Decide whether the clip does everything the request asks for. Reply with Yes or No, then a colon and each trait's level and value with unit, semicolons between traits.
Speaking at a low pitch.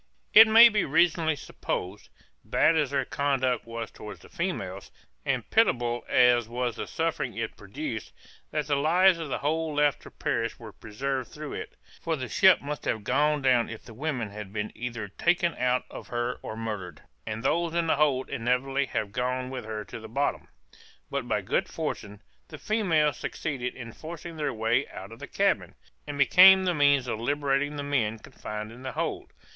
Yes: low, 130 Hz